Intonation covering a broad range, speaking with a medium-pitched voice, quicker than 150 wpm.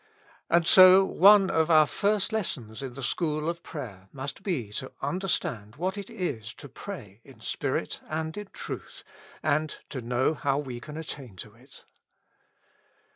Yes: wide, 6.5 semitones; medium, 150 Hz; average, 160 wpm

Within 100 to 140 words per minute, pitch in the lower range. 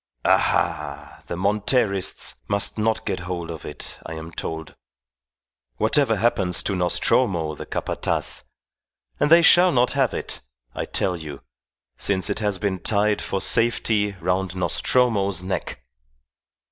Yes: slow, 135 wpm; low, 100 Hz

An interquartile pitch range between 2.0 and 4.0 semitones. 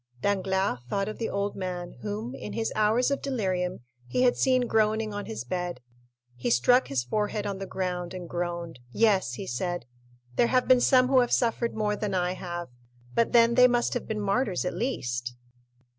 No: average, 4.7 semitones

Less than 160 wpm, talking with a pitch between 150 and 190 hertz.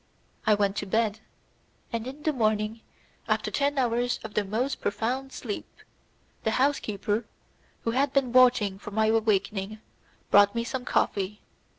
No: average, 150 wpm; high, 225 Hz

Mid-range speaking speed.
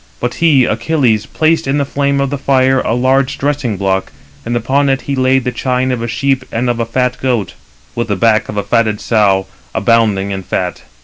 No: fast, 210 wpm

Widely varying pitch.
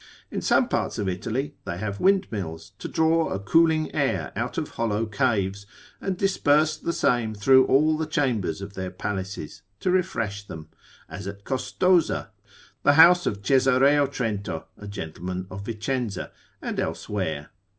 Yes: wide, 7.0 semitones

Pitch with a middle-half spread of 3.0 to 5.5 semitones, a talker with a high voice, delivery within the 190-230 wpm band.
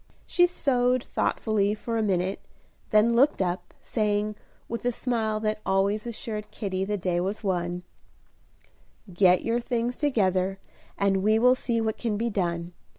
No: average, 3.5 semitones; high, 215 Hz; average, 150 wpm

